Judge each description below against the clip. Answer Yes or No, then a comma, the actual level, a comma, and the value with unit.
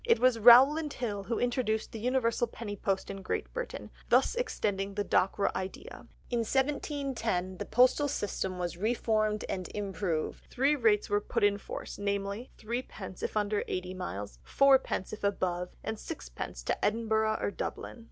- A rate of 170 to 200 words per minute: No, average, 160 wpm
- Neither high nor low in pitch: No, high, 215 Hz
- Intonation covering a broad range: No, average, 4.0 semitones